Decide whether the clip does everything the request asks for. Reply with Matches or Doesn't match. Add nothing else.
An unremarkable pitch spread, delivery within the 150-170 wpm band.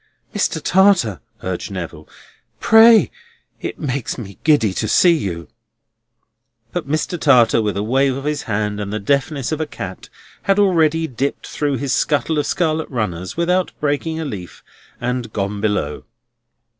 Doesn't match